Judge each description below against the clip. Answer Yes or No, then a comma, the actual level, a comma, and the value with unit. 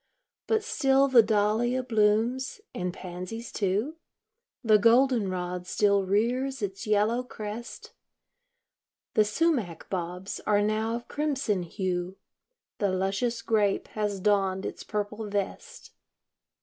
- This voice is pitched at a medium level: No, high, 210 Hz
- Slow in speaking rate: Yes, slow, 115 wpm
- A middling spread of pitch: Yes, average, 3.7 semitones